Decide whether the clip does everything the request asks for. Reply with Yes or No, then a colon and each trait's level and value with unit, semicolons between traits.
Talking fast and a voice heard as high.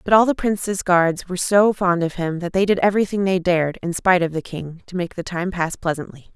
No: fast, 255 wpm; medium, 180 Hz